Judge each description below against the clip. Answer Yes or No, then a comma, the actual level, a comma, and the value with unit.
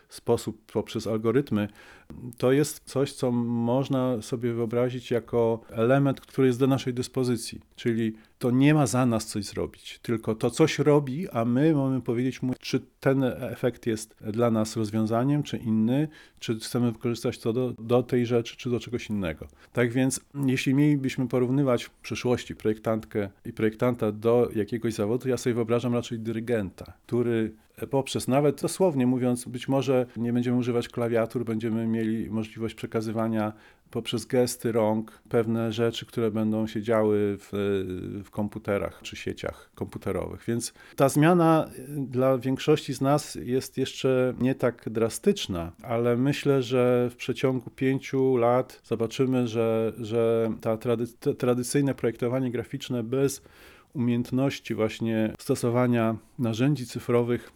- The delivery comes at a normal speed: Yes, average, 140 wpm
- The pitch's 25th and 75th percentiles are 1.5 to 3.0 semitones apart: Yes, narrow, 2.5 semitones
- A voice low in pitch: Yes, low, 120 Hz